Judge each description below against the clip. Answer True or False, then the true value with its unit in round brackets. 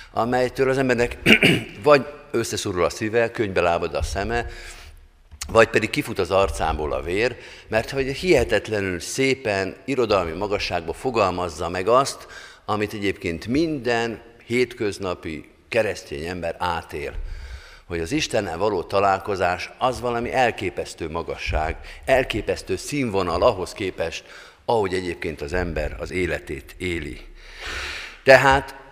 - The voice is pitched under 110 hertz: True (100 Hz)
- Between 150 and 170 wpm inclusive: False (115 wpm)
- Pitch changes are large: True (6.2 semitones)